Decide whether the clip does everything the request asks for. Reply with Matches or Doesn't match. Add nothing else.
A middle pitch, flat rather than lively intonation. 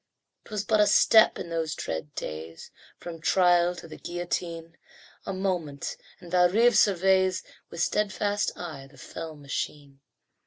Doesn't match